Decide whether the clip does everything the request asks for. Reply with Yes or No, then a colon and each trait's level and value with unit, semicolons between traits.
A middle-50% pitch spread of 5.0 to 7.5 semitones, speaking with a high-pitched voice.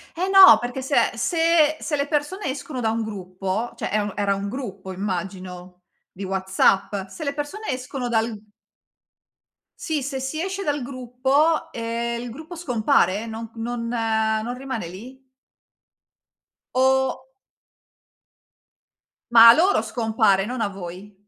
Yes: wide, 5.5 semitones; high, 235 Hz